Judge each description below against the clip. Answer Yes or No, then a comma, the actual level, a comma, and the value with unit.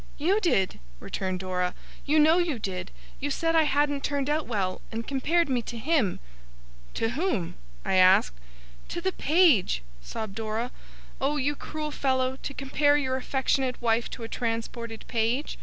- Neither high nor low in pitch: No, very high, 260 Hz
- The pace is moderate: Yes, average, 160 wpm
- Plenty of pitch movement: No, average, 5.0 semitones